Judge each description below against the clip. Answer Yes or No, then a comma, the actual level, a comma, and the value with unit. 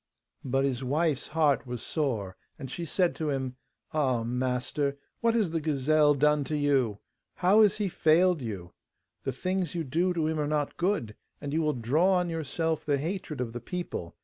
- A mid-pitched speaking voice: Yes, medium, 150 Hz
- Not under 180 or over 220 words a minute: Yes, average, 190 wpm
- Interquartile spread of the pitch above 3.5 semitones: Yes, average, 4.3 semitones